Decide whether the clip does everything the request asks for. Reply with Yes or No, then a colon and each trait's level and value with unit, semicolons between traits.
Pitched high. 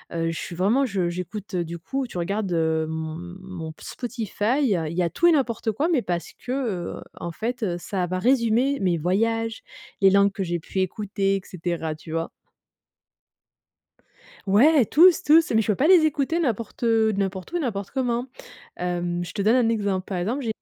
Yes: high, 200 Hz